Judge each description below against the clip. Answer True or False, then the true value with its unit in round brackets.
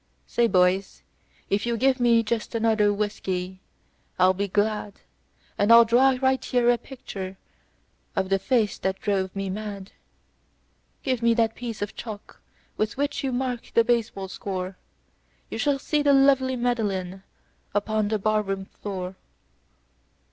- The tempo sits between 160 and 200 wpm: False (145 wpm)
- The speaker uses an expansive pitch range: False (3.7 semitones)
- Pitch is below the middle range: False (215 Hz)